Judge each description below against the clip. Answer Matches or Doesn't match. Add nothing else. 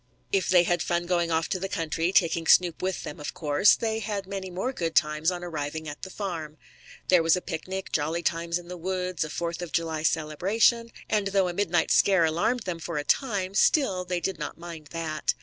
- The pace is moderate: Doesn't match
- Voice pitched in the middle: Matches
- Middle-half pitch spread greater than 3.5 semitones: Doesn't match